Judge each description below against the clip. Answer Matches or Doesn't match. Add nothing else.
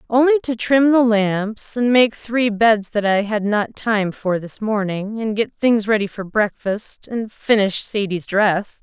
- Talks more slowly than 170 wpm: Doesn't match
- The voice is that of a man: Doesn't match